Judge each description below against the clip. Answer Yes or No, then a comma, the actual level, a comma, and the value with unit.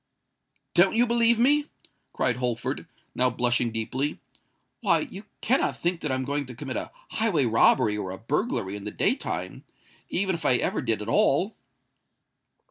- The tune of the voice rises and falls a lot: Yes, wide, 8.5 semitones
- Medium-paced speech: Yes, average, 160 wpm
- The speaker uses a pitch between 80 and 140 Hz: Yes, low, 135 Hz